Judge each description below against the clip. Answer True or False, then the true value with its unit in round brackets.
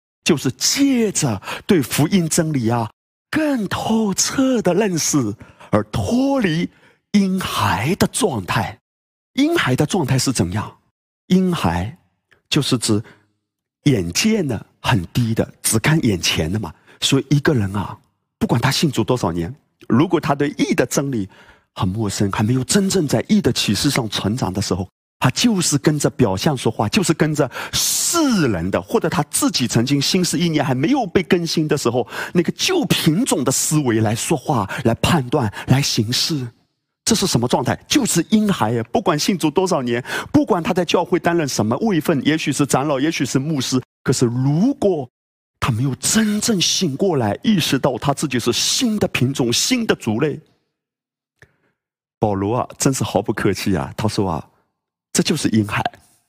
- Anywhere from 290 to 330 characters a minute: False (245 characters per minute)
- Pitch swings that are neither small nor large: False (7.9 semitones)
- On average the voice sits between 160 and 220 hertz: False (140 Hz)